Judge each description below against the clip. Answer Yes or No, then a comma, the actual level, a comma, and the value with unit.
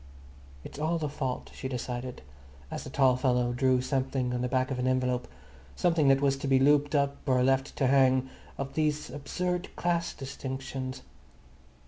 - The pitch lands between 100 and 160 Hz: Yes, low, 135 Hz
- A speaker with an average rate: Yes, average, 170 wpm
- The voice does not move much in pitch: Yes, narrow, 1.9 semitones